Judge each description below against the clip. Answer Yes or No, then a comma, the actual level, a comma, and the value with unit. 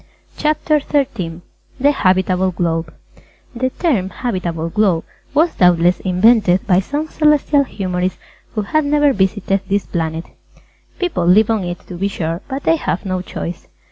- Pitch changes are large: Yes, wide, 7.2 semitones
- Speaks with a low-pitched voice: No, high, 190 Hz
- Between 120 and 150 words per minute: Yes, average, 145 wpm